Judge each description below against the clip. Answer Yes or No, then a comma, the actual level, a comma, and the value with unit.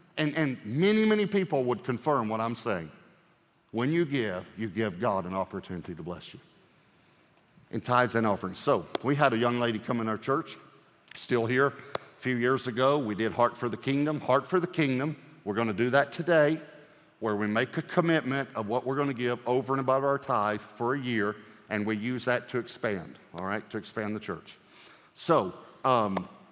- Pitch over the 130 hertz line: No, low, 125 Hz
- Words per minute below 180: No, fast, 205 wpm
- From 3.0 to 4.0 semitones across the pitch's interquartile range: No, average, 4.5 semitones